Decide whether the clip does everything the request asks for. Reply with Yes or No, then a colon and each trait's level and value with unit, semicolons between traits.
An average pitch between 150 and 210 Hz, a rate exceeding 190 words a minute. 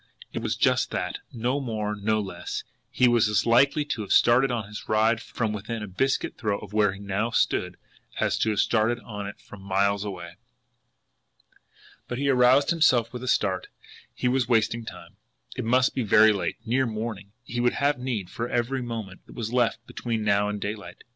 No: low, 110 Hz; average, 200 wpm